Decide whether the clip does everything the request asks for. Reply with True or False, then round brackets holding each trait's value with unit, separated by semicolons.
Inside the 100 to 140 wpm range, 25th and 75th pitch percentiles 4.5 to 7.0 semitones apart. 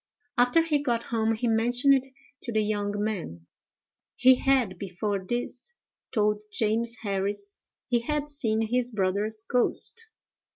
False (135 wpm; 3.3 semitones)